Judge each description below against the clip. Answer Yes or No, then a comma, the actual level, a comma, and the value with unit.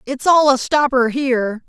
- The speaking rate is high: No, average, 180 wpm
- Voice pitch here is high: Yes, very high, 260 Hz